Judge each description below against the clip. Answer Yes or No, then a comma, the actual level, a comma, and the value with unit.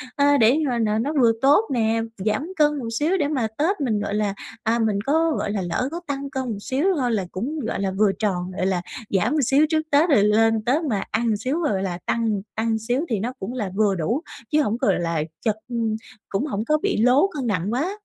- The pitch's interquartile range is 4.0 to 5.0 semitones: No, wide, 5.6 semitones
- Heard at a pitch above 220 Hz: Yes, high, 230 Hz